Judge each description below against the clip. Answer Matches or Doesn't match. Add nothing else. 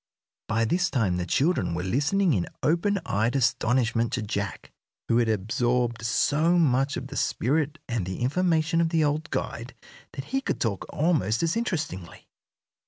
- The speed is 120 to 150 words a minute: Doesn't match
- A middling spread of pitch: Doesn't match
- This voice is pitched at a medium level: Doesn't match